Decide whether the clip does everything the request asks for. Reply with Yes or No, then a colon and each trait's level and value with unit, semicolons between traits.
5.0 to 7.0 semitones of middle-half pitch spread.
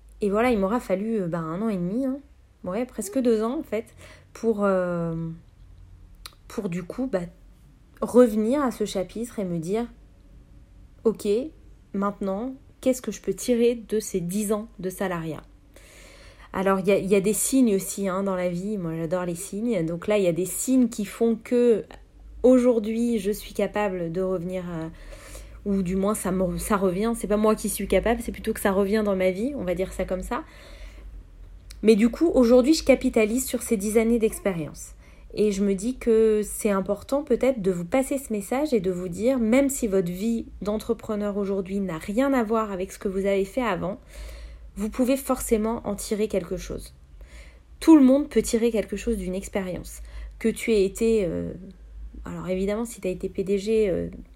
No: average, 3.8 semitones